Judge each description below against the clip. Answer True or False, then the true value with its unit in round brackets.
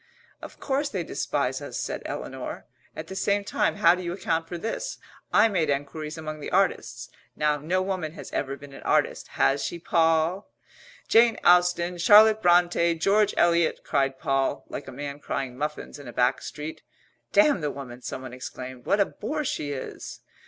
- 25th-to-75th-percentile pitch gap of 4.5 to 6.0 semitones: True (5.1 semitones)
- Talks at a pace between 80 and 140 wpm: False (180 wpm)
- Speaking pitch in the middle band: True (165 Hz)